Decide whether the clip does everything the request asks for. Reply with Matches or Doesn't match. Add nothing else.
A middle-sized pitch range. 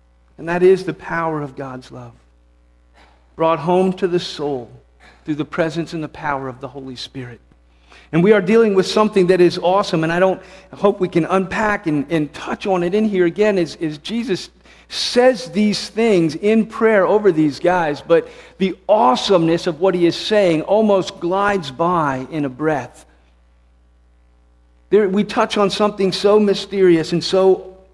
Doesn't match